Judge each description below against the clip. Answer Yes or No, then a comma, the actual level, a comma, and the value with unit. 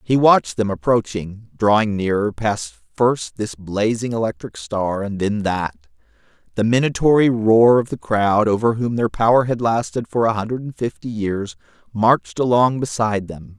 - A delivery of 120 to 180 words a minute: Yes, average, 165 wpm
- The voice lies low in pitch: Yes, low, 110 Hz